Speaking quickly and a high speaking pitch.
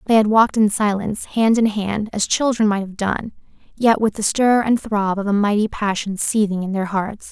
Yes: fast, 220 wpm; high, 210 Hz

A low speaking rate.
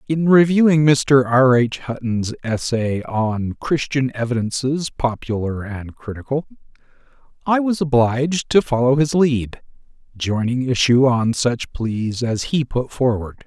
Yes: slow, 130 wpm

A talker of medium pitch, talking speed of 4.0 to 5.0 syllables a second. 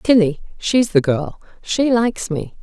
No: high, 195 Hz; 4.2 syllables/s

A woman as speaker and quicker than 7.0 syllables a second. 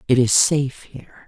No: female; 5.6 syllables/s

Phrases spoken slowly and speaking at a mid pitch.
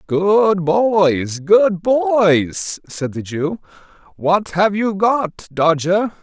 Yes: slow, 115 wpm; medium, 180 Hz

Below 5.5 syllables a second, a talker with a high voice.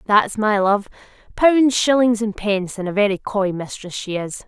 Yes: 4.7 syllables/s; high, 210 Hz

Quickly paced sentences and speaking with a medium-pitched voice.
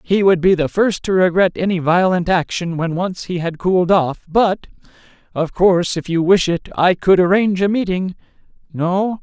No: average, 190 wpm; medium, 180 Hz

